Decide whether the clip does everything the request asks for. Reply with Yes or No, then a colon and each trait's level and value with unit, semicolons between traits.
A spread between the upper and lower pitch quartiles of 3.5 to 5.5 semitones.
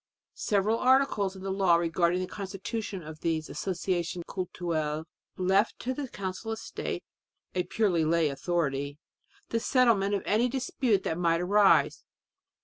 Yes: average, 3.9 semitones